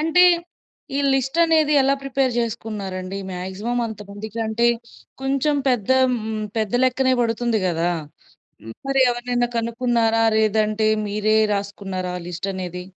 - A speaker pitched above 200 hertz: Yes, high, 225 Hz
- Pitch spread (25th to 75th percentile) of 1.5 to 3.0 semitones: No, average, 3.7 semitones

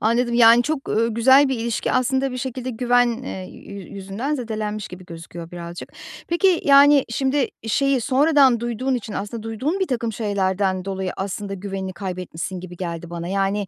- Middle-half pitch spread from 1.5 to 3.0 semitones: No, average, 5.2 semitones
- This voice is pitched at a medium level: No, high, 225 Hz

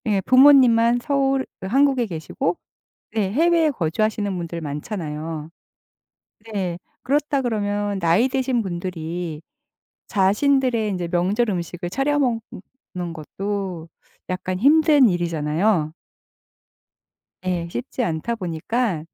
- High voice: Yes, high, 200 Hz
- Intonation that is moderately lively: No, wide, 6.5 semitones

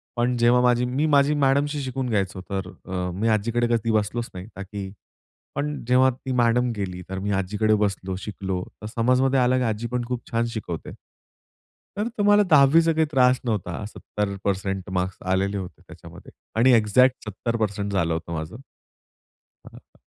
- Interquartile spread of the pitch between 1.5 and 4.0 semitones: No, average, 4.7 semitones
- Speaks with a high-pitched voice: No, low, 110 Hz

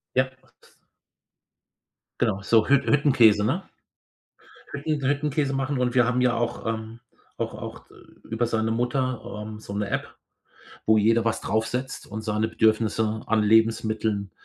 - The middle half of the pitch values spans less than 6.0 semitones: Yes, average, 2.9 semitones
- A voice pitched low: Yes, low, 115 Hz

